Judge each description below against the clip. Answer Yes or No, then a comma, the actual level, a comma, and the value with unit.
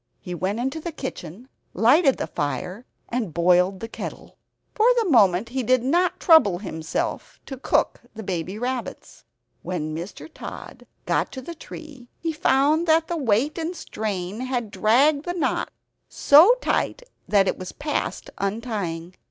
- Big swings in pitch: Yes, wide, 8.2 semitones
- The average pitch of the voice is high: Yes, high, 240 Hz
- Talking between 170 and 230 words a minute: No, average, 155 wpm